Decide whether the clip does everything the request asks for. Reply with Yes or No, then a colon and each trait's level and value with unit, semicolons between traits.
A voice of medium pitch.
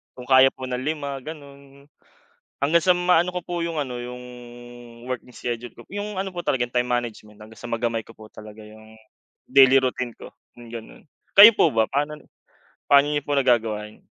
No: low, 130 Hz